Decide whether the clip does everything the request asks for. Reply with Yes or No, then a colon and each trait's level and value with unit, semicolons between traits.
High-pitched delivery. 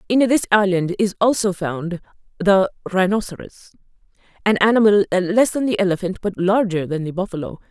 Yes: high, 195 Hz